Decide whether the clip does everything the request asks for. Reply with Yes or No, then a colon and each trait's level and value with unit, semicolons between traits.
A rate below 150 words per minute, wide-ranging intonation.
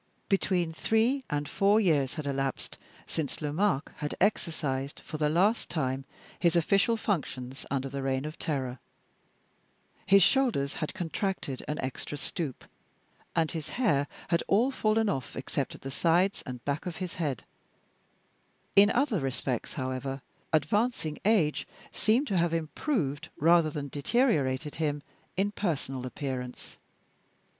Yes: average, 140 wpm; wide, 6.3 semitones